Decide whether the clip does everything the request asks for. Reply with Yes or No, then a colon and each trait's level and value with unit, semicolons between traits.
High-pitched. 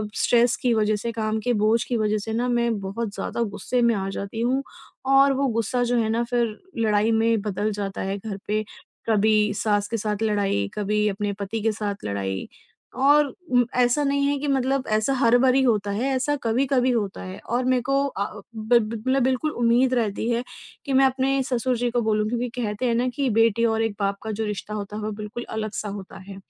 Yes: high, 225 Hz